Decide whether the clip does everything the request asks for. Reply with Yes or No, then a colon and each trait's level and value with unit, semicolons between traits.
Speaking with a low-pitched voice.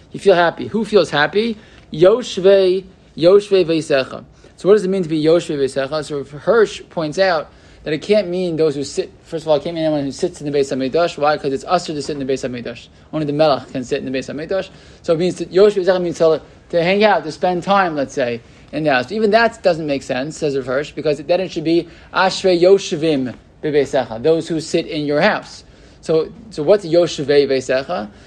No: medium, 160 Hz